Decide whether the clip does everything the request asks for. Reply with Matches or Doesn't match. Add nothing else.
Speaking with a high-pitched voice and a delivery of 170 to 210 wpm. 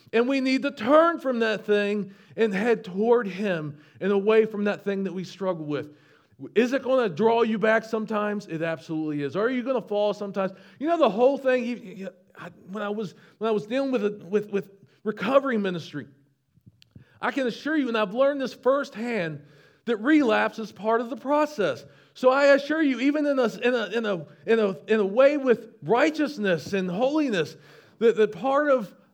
Matches